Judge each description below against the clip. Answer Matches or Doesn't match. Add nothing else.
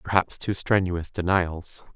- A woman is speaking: Doesn't match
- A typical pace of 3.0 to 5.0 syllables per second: Matches